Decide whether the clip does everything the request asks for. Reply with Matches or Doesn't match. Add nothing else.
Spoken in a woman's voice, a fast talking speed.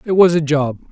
Doesn't match